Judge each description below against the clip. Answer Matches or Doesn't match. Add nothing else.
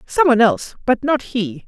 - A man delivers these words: Doesn't match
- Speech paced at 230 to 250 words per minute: Doesn't match